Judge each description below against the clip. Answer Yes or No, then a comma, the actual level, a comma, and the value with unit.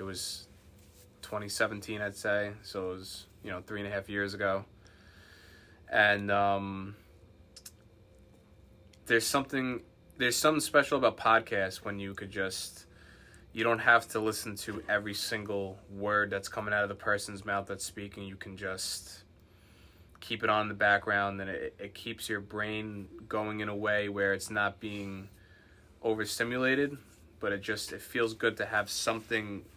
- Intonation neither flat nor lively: No, narrow, 1.8 semitones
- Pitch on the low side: Yes, low, 100 Hz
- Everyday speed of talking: Yes, average, 160 wpm